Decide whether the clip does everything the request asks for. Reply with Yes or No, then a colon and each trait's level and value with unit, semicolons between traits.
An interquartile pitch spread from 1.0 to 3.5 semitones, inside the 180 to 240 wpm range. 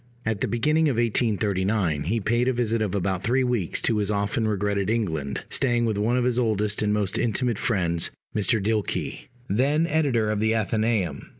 Yes: average, 2.9 semitones; average, 185 wpm